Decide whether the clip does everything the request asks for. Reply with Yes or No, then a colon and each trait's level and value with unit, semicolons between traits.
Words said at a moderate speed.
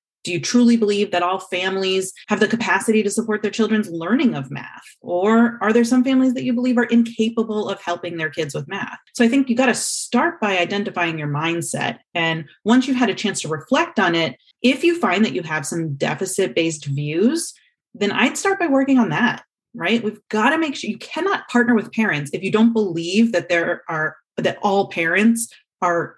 No: fast, 210 wpm